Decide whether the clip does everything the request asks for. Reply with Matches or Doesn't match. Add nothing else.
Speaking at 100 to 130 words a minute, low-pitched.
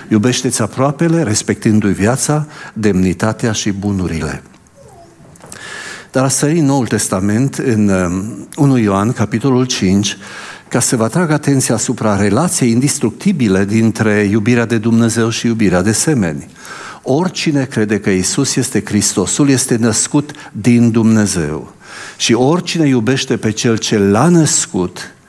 Matches